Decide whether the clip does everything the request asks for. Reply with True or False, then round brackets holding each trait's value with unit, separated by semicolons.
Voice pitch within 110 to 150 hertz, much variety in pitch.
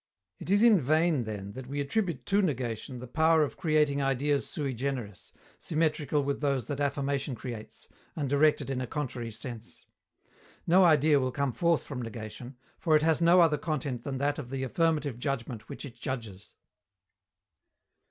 False (140 Hz; 3.7 semitones)